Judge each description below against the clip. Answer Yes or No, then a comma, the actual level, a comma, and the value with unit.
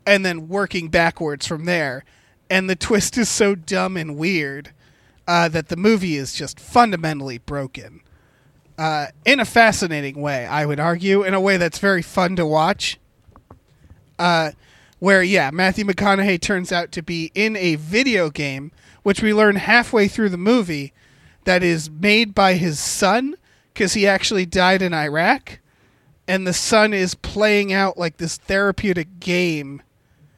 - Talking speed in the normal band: Yes, average, 160 wpm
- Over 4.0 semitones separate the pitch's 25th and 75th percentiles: Yes, average, 4.7 semitones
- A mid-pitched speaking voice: Yes, medium, 180 Hz